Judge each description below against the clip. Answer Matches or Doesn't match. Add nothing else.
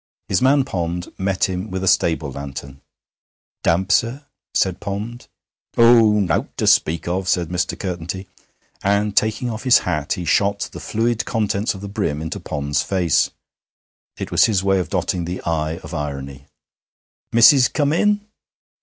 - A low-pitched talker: Matches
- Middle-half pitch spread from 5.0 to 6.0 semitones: Doesn't match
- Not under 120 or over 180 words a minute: Matches